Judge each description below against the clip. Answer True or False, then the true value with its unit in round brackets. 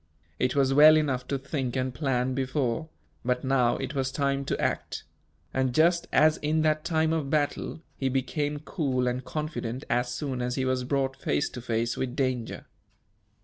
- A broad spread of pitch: False (3.0 semitones)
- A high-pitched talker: False (135 Hz)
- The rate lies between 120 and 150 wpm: False (180 wpm)